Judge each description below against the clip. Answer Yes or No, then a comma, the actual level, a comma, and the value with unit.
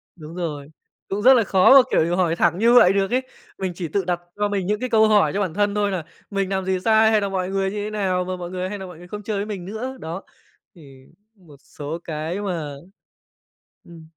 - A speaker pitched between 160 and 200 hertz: Yes, high, 190 Hz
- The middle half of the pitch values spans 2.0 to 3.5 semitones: Yes, average, 3.2 semitones